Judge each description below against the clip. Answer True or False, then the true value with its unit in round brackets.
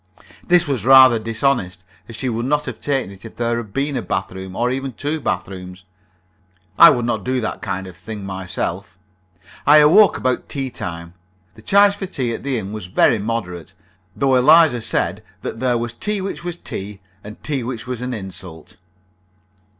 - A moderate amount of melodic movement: False (5.9 semitones)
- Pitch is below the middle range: True (120 Hz)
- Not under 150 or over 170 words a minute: False (190 wpm)